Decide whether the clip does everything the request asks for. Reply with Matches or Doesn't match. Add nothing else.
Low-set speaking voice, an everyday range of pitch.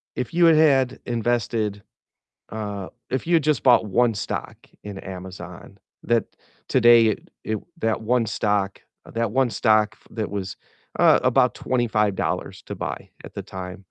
Matches